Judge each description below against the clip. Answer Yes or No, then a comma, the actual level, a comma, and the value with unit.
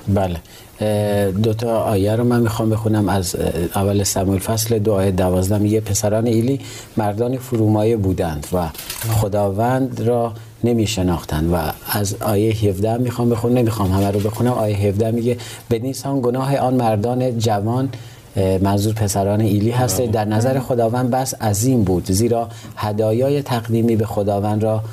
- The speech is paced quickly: No, average, 140 wpm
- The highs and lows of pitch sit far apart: No, average, 2.7 semitones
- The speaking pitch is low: Yes, low, 110 Hz